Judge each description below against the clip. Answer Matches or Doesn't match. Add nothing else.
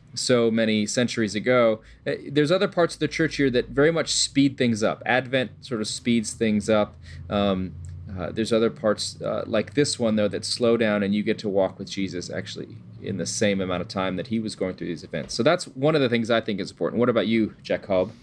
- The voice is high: Doesn't match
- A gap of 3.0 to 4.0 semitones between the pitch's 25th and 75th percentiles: Matches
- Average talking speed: Doesn't match